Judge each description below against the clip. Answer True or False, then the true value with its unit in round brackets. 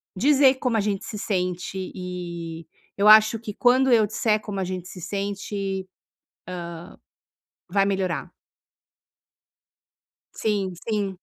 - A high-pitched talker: True (200 Hz)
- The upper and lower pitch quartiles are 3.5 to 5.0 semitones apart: False (2.8 semitones)